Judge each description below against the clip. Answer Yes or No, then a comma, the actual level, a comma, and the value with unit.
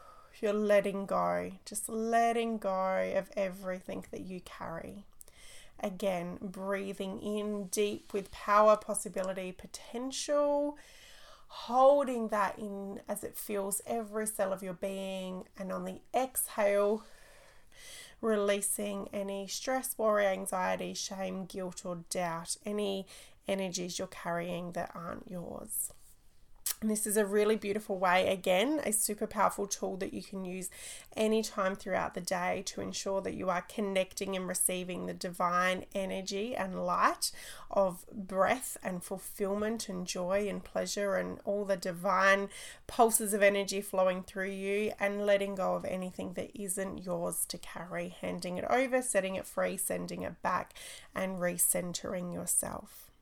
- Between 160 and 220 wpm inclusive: No, average, 140 wpm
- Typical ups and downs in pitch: No, narrow, 2.1 semitones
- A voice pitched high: Yes, high, 195 Hz